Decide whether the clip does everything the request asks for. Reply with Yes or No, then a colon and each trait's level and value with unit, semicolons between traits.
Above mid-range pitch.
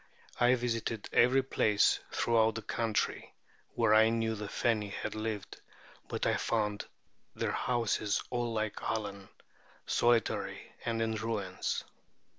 No: low, 110 Hz